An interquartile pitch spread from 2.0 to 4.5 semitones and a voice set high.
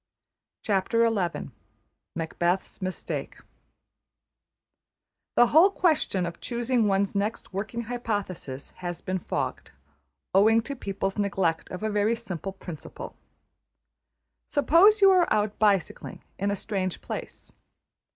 Yes: average, 3.9 semitones; high, 200 Hz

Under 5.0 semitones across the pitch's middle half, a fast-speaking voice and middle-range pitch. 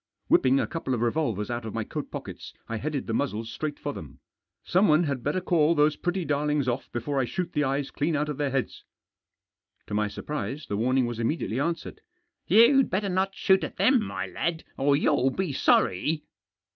No: wide, 5.5 semitones; fast, 210 wpm; medium, 145 Hz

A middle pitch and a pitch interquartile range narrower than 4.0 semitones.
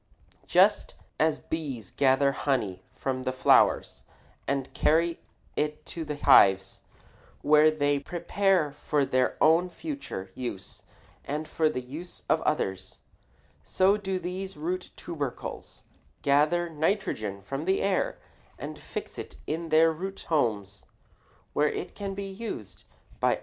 No: medium, 150 Hz; average, 4.8 semitones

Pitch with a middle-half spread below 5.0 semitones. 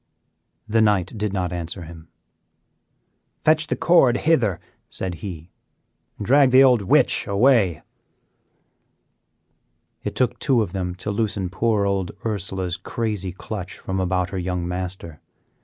Yes: average, 4.0 semitones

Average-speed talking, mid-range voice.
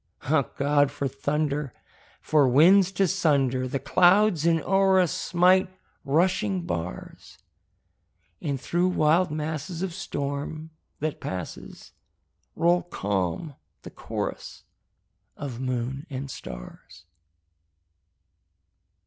No: slow, 100 wpm; medium, 150 Hz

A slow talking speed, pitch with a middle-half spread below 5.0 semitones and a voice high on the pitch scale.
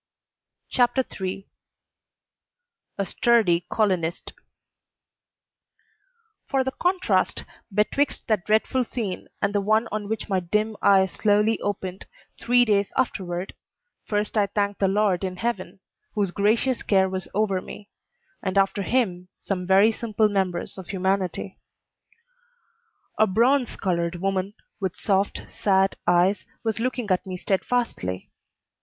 Yes: slow, 125 wpm; narrow, 2.6 semitones; high, 200 Hz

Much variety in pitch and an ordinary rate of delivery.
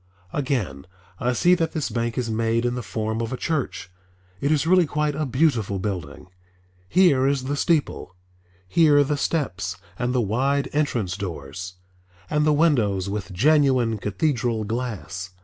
Yes: wide, 6.4 semitones; average, 155 wpm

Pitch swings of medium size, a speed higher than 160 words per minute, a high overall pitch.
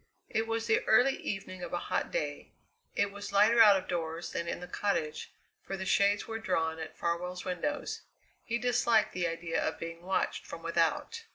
Yes: average, 4.7 semitones; average, 190 wpm; high, 195 Hz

